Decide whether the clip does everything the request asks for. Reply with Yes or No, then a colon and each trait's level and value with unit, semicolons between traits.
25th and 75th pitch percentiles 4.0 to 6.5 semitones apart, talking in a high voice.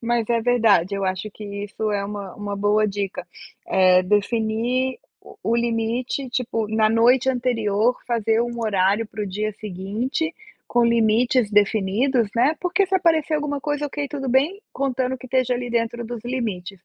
No: average, 3.6 semitones; high, 230 Hz